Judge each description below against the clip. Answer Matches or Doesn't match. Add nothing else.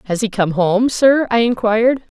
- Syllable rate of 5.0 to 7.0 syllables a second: Doesn't match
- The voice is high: Matches